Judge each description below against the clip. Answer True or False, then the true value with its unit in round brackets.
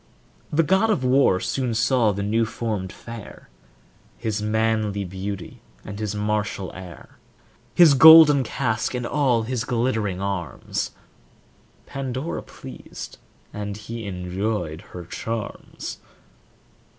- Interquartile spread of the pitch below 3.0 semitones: False (4.0 semitones)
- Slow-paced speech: True (115 wpm)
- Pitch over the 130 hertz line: False (110 Hz)